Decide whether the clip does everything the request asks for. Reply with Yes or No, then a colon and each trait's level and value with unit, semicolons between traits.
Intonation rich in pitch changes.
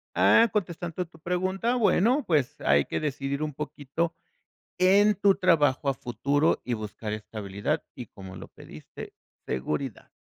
Yes: wide, 7.2 semitones